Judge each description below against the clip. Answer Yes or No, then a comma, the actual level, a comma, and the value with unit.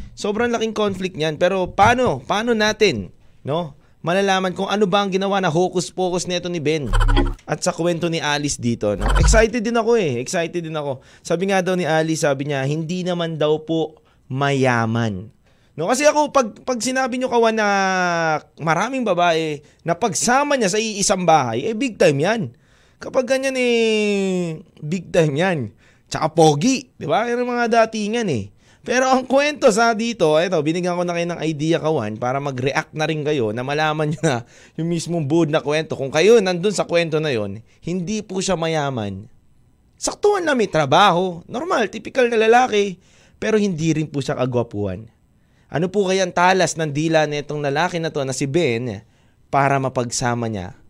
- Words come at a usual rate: No, fast, 175 wpm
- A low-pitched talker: No, medium, 170 Hz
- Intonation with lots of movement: Yes, wide, 6.3 semitones